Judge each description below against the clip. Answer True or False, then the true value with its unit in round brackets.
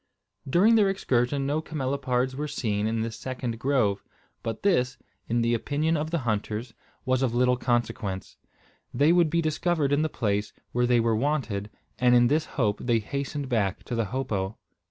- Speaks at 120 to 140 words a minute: False (175 wpm)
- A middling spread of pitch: True (4.2 semitones)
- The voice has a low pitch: True (125 Hz)